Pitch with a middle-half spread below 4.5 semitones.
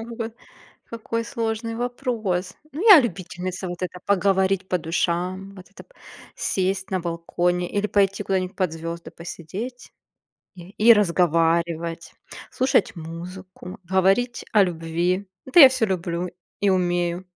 Yes: average, 3.5 semitones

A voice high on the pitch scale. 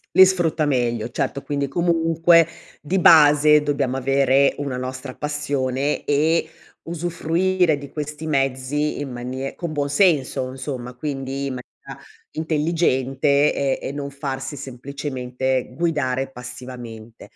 No: medium, 140 Hz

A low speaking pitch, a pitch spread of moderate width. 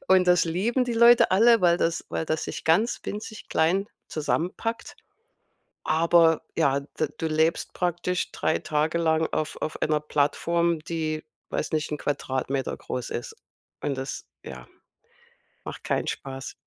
No: medium, 160 Hz; average, 3.1 semitones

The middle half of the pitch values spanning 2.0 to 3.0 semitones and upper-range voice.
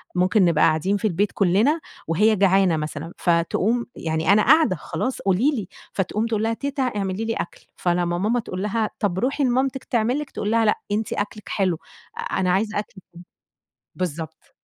No: average, 4.3 semitones; high, 205 Hz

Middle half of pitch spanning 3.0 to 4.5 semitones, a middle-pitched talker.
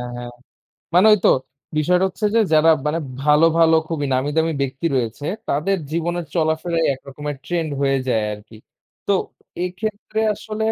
Yes: average, 4.1 semitones; medium, 160 Hz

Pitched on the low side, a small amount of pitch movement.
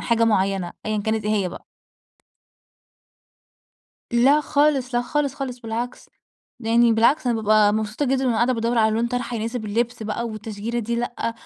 No: high, 230 Hz; narrow, 2.2 semitones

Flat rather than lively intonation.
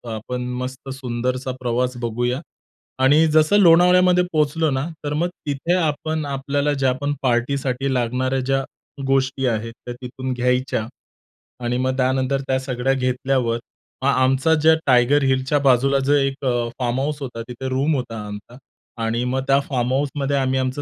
Yes: narrow, 2.1 semitones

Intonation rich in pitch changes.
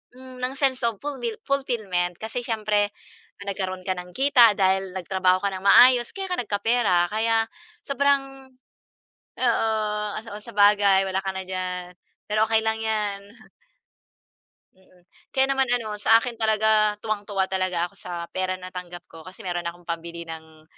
No: average, 3.7 semitones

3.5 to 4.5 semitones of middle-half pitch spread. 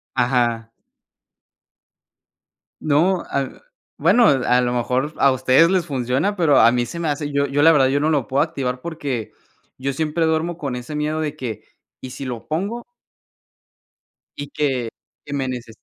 Yes: average, 3.9 semitones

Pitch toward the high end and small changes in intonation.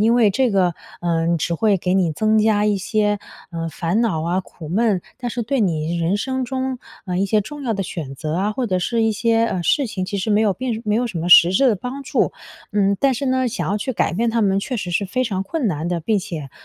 No: high, 205 Hz; average, 4.7 semitones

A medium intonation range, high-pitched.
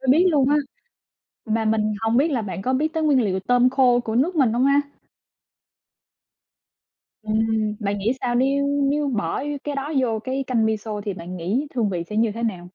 Yes: average, 4.1 semitones; high, 235 Hz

